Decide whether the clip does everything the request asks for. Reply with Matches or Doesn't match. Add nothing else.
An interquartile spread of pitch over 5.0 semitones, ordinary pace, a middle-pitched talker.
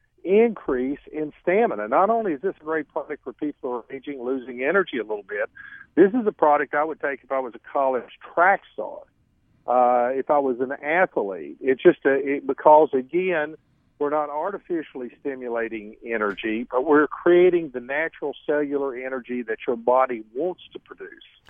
Matches